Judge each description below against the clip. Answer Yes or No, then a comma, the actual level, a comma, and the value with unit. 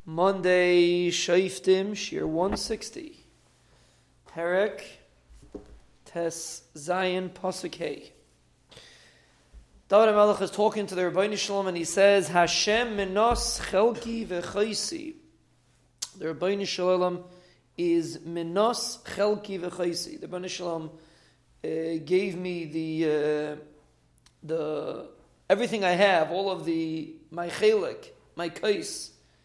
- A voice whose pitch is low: No, medium, 180 Hz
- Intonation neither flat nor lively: Yes, average, 3.4 semitones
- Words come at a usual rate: No, slow, 100 wpm